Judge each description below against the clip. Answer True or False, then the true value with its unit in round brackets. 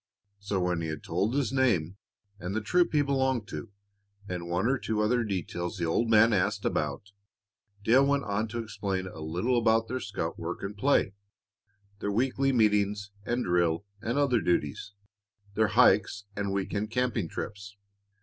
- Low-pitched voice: True (105 Hz)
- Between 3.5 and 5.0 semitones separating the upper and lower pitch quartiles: True (4.1 semitones)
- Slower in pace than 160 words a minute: False (170 wpm)